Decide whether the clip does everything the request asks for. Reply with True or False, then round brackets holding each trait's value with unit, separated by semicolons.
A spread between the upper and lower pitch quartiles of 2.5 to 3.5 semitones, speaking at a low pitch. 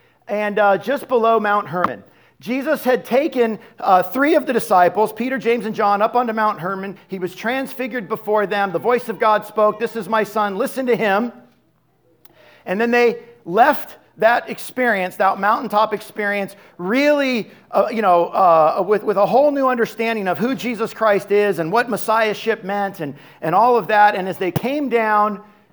False (3.0 semitones; 215 Hz)